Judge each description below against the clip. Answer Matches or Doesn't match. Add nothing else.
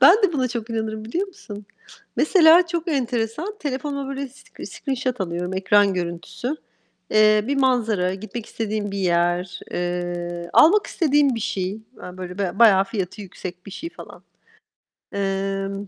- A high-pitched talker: Matches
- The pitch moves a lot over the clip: Matches